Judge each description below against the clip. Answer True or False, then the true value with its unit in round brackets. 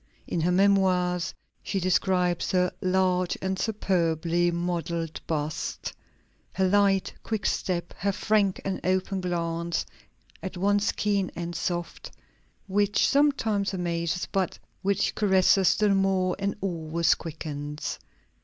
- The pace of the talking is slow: True (115 wpm)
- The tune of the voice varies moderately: False (2.3 semitones)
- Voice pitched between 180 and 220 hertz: True (185 Hz)